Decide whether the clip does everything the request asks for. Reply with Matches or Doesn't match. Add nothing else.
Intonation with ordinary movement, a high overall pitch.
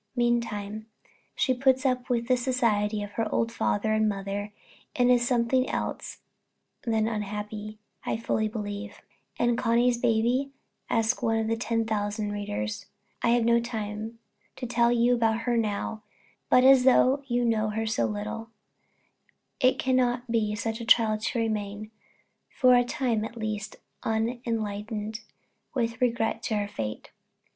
Doesn't match